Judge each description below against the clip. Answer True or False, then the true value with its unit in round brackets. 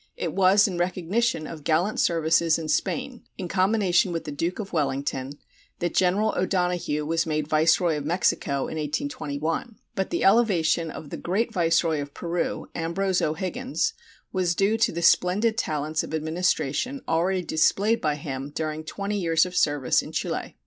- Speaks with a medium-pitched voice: True (170 Hz)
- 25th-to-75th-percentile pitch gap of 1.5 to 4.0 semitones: True (3.7 semitones)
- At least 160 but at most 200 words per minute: True (165 wpm)